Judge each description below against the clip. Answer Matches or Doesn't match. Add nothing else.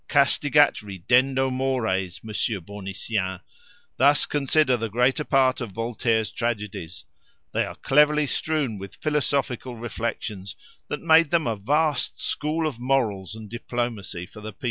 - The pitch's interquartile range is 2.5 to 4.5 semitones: Doesn't match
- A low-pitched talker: Matches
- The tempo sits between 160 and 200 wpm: Doesn't match